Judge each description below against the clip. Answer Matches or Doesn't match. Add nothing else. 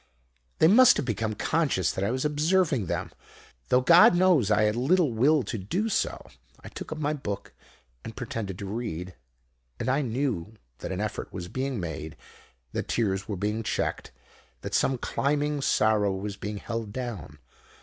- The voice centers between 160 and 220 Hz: Doesn't match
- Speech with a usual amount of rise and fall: Doesn't match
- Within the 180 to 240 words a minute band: Doesn't match